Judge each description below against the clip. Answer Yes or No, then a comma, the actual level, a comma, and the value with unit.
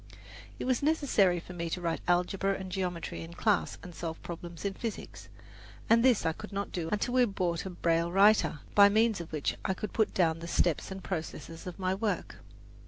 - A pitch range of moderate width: Yes, average, 3.4 semitones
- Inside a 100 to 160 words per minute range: No, fast, 205 wpm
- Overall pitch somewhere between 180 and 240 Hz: Yes, medium, 185 Hz